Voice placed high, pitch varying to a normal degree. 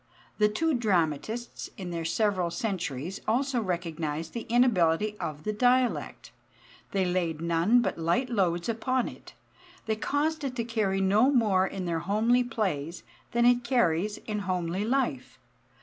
No: high, 210 Hz; wide, 5.7 semitones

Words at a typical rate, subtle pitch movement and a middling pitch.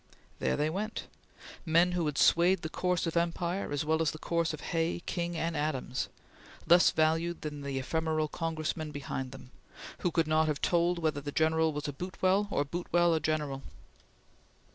Yes: average, 180 wpm; narrow, 2.2 semitones; medium, 160 Hz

